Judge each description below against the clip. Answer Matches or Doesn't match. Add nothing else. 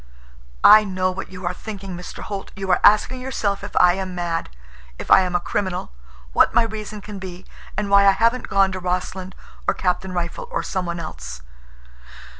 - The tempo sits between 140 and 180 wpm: Doesn't match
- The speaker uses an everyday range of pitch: Doesn't match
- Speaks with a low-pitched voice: Doesn't match